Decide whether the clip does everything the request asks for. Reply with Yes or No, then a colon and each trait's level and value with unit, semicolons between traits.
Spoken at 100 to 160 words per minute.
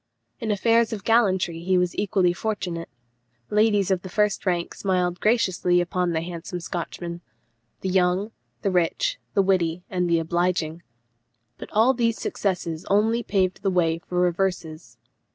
Yes: average, 150 wpm